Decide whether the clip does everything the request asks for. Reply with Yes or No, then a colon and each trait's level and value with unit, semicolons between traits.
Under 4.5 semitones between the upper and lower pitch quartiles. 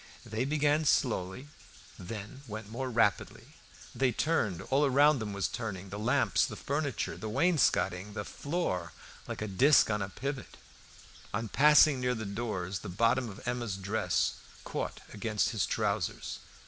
No: average, 5.1 semitones